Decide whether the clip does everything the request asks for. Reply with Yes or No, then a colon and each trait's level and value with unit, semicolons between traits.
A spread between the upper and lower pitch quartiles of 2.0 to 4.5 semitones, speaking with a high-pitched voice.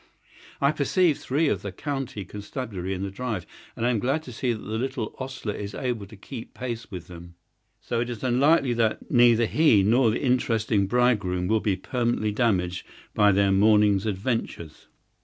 No: average, 4.0 semitones; low, 115 Hz